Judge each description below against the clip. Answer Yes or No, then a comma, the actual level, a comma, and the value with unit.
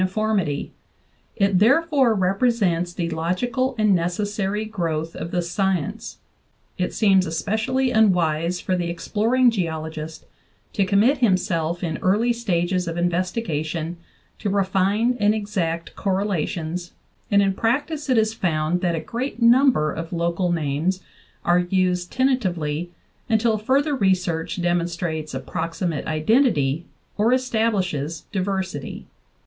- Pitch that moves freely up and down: No, average, 4.5 semitones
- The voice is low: No, medium, 185 Hz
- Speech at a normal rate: No, slow, 120 wpm